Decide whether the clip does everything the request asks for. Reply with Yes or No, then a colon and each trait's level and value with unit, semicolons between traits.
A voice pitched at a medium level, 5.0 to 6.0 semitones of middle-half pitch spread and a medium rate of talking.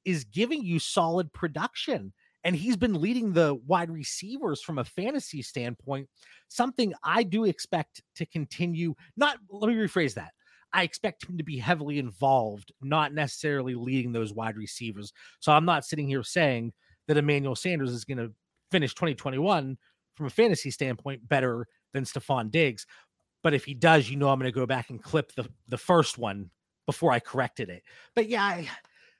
Yes: medium, 145 Hz; wide, 5.4 semitones; average, 175 wpm